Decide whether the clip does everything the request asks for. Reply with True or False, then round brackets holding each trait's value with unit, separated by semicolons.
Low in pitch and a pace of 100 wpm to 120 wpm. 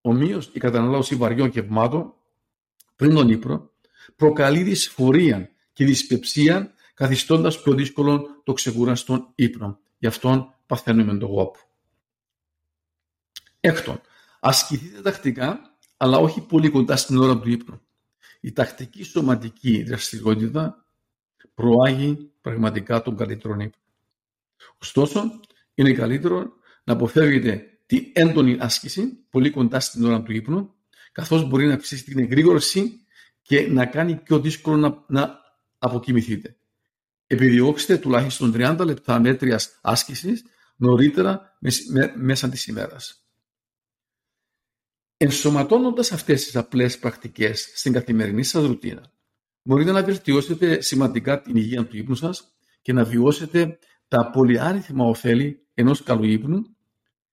True (130 Hz; 115 wpm)